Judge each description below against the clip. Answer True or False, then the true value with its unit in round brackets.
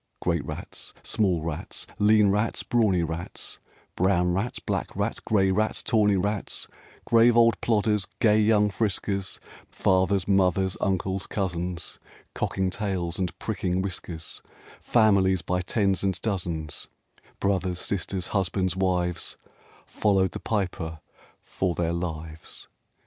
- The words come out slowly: True (120 wpm)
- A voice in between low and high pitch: False (95 Hz)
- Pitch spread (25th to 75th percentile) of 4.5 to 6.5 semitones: False (2.7 semitones)